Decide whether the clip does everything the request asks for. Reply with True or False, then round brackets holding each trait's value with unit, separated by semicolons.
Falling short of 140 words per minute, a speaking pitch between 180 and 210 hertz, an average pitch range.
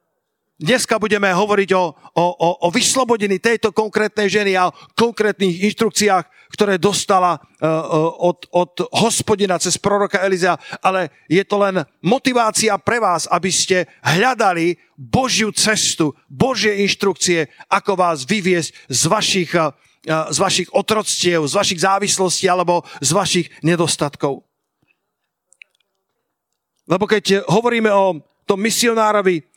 True (115 wpm; 190 Hz; 3.5 semitones)